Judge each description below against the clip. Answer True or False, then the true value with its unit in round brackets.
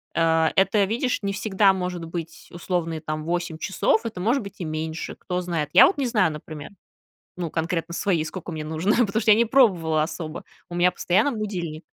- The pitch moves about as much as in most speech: True (3.9 semitones)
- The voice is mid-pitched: True (175 Hz)